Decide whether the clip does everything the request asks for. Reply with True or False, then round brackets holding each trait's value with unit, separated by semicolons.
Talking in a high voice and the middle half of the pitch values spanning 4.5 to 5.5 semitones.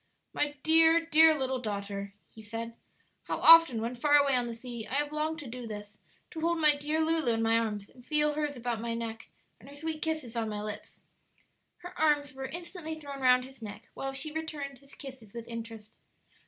True (265 Hz; 5.1 semitones)